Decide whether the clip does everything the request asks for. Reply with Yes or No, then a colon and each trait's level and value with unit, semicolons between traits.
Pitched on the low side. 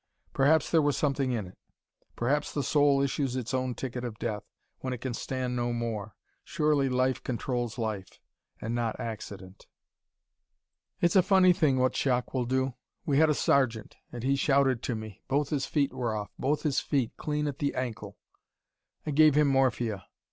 Yes: low, 130 Hz